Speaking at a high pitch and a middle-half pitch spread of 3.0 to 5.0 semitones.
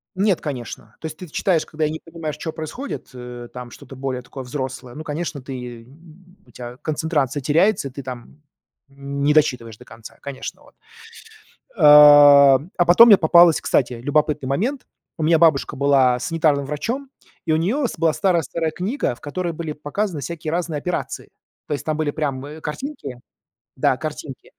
No: medium, 150 Hz; average, 3.6 semitones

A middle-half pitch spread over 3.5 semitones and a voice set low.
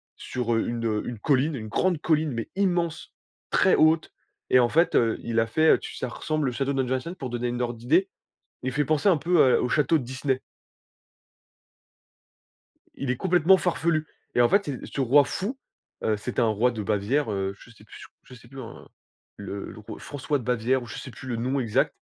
Yes: average, 4.7 semitones; low, 130 Hz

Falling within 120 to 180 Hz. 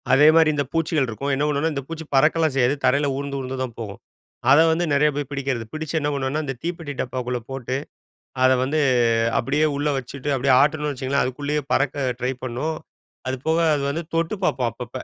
Yes: medium, 140 Hz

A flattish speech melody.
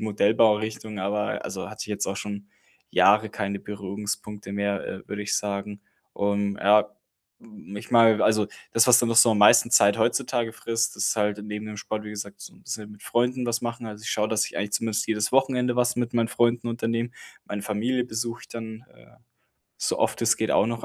Yes: narrow, 2.2 semitones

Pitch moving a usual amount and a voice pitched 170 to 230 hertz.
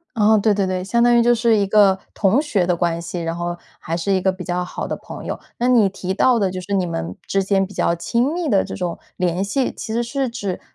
Yes: average, 4.3 semitones; high, 195 Hz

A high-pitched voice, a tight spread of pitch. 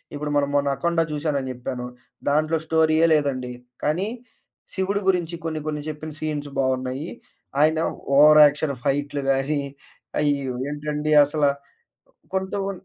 No: medium, 150 Hz; narrow, 1.9 semitones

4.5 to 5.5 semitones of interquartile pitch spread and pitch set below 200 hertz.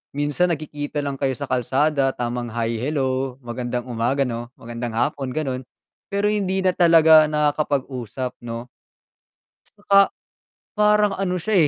Yes: average, 5.1 semitones; medium, 140 Hz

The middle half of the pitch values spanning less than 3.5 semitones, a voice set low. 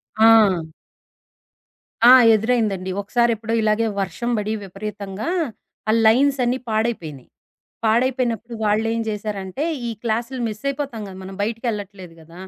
No: average, 2.9 semitones; high, 220 Hz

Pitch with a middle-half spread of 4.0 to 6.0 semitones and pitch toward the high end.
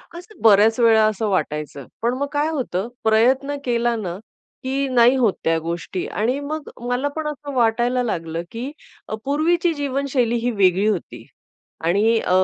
Yes: average, 4.9 semitones; high, 235 Hz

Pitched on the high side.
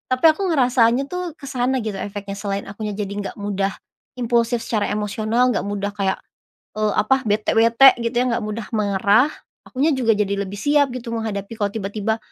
Yes: high, 220 Hz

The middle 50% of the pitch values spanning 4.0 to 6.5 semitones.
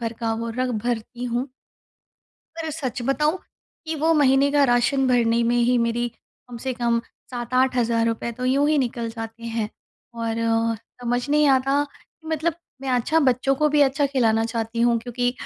No: average, 2.9 semitones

